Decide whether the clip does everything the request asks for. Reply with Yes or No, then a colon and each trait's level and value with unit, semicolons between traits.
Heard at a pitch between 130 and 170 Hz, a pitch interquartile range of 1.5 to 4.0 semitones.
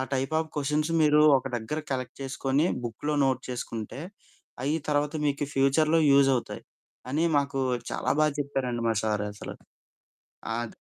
Yes: medium, 140 Hz; average, 2.9 semitones